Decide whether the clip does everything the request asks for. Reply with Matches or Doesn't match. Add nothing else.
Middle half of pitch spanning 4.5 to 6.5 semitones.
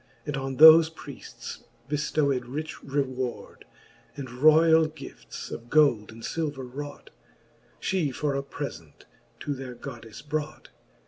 Doesn't match